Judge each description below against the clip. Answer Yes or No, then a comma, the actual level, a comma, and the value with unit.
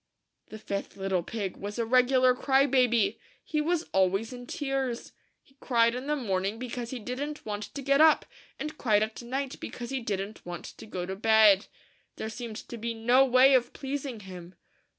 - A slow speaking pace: No, average, 190 wpm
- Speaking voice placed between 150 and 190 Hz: No, high, 235 Hz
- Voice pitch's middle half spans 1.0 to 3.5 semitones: No, average, 4.2 semitones